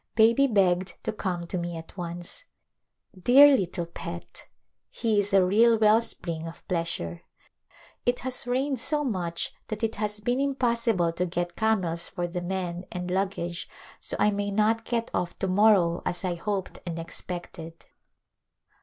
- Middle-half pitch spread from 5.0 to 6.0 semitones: No, average, 4.3 semitones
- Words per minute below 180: Yes, average, 160 wpm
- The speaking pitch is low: No, high, 190 Hz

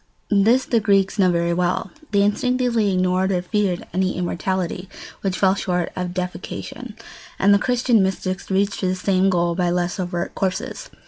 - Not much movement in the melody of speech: Yes, narrow, 2.0 semitones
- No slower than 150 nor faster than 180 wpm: Yes, average, 160 wpm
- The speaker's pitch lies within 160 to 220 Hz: Yes, high, 190 Hz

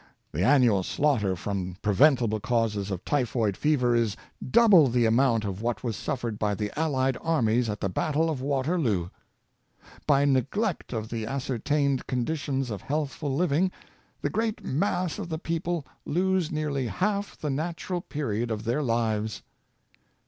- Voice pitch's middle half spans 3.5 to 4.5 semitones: No, wide, 5.6 semitones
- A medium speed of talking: Yes, average, 150 wpm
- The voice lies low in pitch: Yes, low, 130 Hz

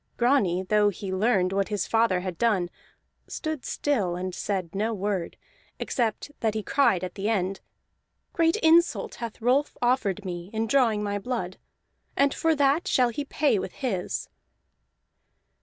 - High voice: Yes, high, 210 Hz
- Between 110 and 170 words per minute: Yes, average, 155 wpm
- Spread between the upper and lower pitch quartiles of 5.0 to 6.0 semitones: Yes, average, 5.3 semitones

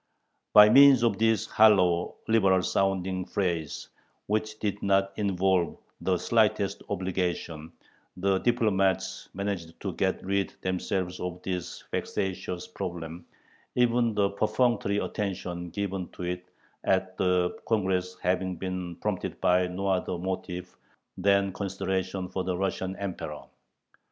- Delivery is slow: Yes, slow, 120 wpm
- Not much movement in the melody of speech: Yes, narrow, 1.7 semitones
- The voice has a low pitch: Yes, very low, 95 Hz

